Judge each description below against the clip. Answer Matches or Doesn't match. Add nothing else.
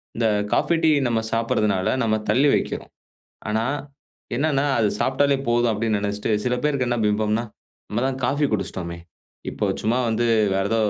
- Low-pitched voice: Matches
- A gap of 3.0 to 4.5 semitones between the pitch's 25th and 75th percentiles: Matches